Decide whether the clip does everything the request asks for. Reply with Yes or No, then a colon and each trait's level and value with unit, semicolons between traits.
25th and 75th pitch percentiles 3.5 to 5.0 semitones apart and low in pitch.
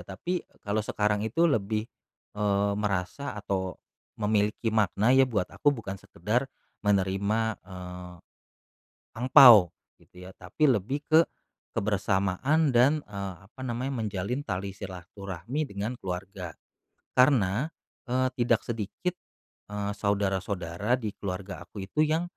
Yes: average, 4.4 semitones; low, 105 Hz